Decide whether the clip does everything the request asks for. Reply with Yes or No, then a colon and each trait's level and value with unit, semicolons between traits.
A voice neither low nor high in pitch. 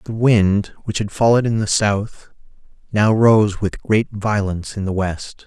No: low, 105 Hz